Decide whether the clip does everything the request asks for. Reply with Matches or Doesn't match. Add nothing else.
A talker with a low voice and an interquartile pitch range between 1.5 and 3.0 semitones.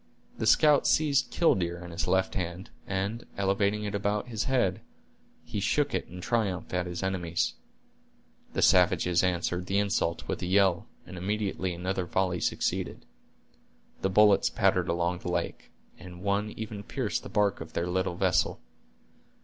Matches